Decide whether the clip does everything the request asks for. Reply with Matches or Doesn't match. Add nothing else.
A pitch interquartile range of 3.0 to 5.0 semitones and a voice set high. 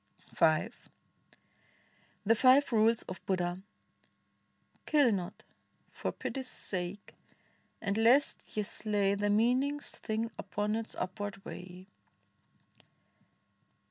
Matches